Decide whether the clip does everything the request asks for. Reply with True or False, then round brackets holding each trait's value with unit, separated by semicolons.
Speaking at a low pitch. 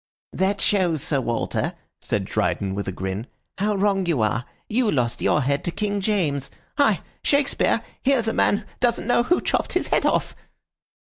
False (190 Hz)